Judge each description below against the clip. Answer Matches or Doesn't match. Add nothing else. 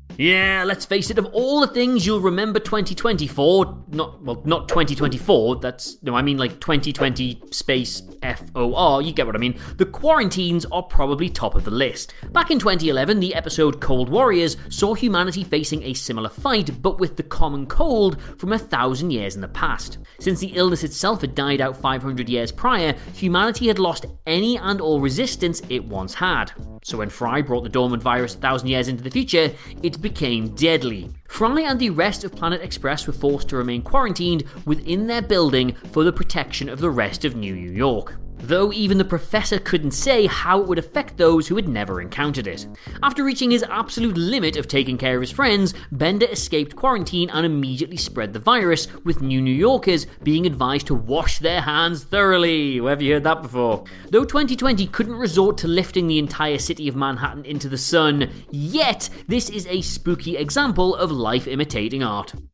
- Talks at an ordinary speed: Matches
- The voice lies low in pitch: Doesn't match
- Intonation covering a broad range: Matches